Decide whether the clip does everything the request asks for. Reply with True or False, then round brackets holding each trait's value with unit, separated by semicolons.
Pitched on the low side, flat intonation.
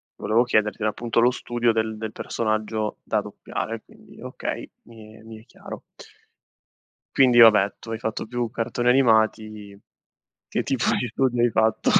True (110 Hz; 1.8 semitones)